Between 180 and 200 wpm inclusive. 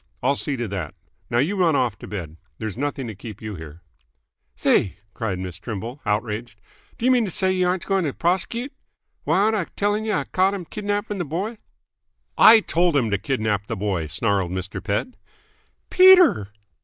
Yes: average, 185 wpm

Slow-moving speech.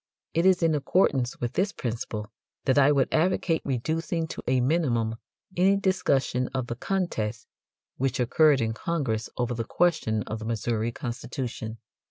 No: average, 155 wpm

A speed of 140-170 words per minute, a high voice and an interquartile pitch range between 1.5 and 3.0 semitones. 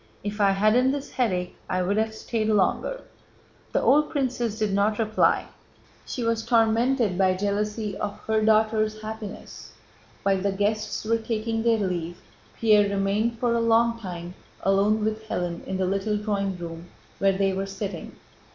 Yes: average, 160 wpm; high, 215 Hz; narrow, 2.5 semitones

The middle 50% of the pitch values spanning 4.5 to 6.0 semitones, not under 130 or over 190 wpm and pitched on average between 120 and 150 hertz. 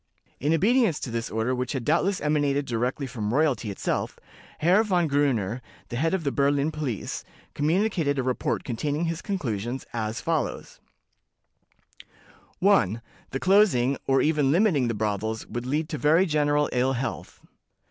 Yes: average, 4.9 semitones; average, 150 wpm; medium, 140 Hz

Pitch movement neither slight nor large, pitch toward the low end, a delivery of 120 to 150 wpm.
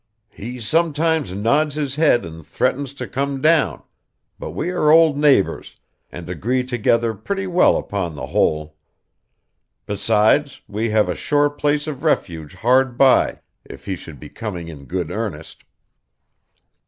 No: wide, 7.8 semitones; low, 120 Hz; average, 145 wpm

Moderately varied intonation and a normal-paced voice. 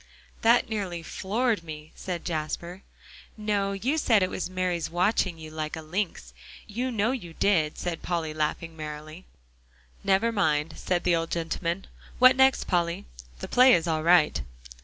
Yes: average, 4.2 semitones; average, 160 wpm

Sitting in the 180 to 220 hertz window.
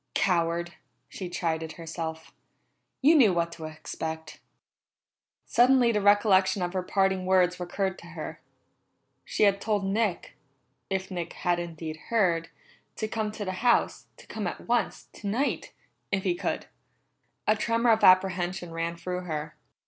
Yes: medium, 185 Hz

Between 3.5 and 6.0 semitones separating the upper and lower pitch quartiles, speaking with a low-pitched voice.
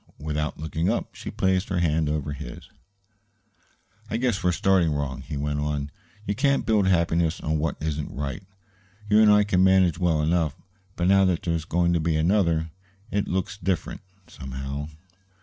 Yes: average, 3.9 semitones; very low, 85 Hz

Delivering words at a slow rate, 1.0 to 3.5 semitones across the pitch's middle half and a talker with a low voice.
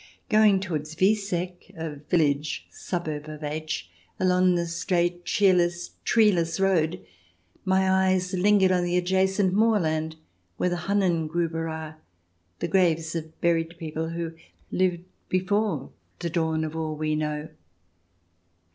No: slow, 130 wpm; average, 2.9 semitones; medium, 170 Hz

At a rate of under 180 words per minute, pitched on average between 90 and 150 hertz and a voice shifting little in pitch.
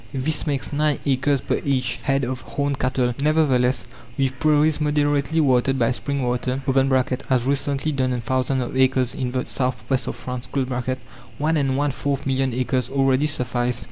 Yes: average, 165 wpm; low, 135 Hz; narrow, 2.1 semitones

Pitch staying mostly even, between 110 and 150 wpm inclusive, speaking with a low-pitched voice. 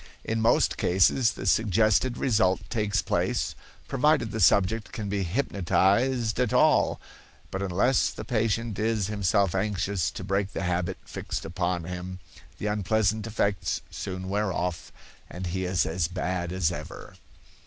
No: average, 3.2 semitones; average, 145 wpm; low, 100 Hz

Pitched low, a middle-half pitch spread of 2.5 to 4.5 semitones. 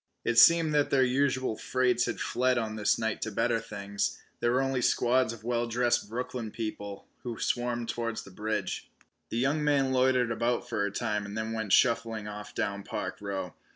Yes: low, 115 Hz; average, 2.8 semitones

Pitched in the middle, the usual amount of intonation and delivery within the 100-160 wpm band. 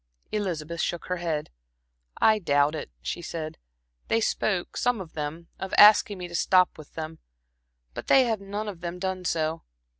No: medium, 175 Hz; average, 3.8 semitones; average, 175 wpm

